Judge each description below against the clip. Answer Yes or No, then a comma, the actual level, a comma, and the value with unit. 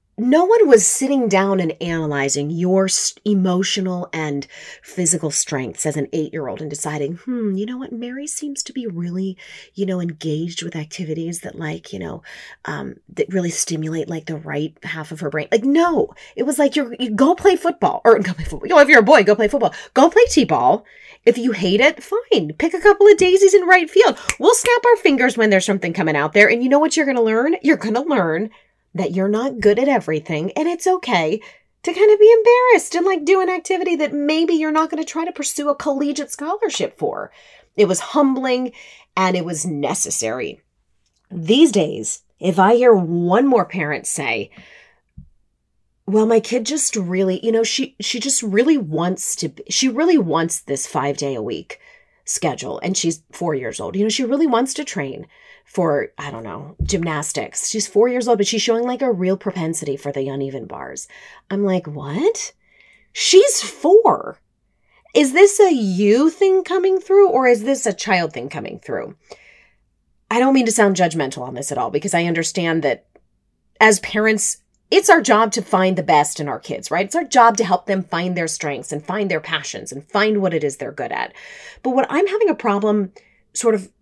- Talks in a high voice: Yes, high, 220 Hz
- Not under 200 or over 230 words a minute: Yes, fast, 205 wpm